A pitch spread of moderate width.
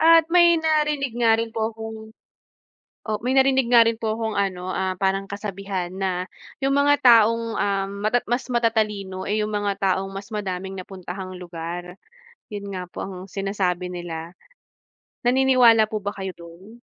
Yes: average, 3.6 semitones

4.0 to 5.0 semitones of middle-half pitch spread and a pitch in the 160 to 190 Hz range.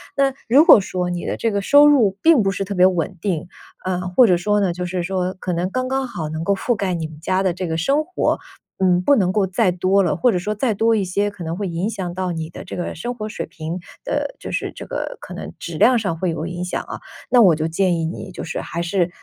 No: average, 3.3 semitones; medium, 185 Hz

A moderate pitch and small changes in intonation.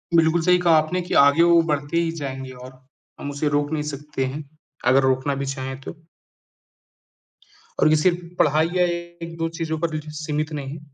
No: medium, 155 Hz; average, 3.2 semitones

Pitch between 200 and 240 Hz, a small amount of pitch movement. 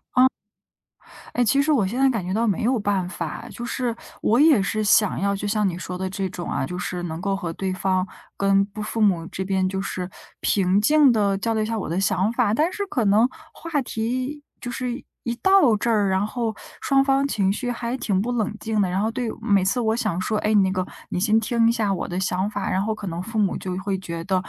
No: high, 210 Hz; average, 3.8 semitones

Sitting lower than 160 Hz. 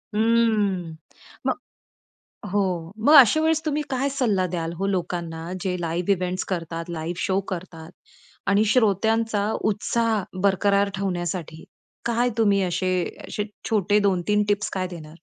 No: high, 195 Hz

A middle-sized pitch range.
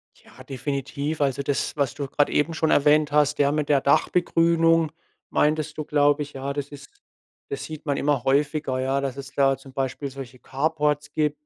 No: narrow, 1.7 semitones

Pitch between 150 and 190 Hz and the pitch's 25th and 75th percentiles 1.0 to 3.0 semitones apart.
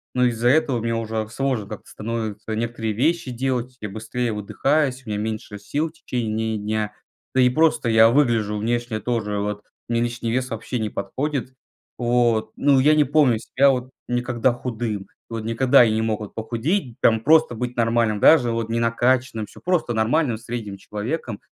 No: low, 115 Hz; average, 2.7 semitones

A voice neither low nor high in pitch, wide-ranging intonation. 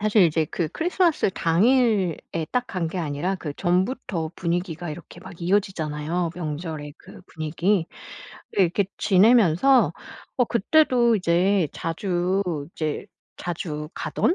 No: medium, 180 Hz; average, 4.0 semitones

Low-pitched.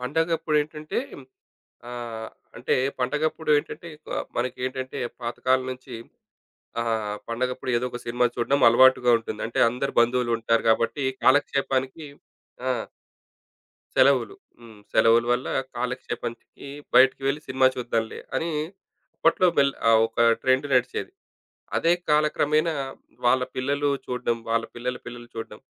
Yes: low, 125 Hz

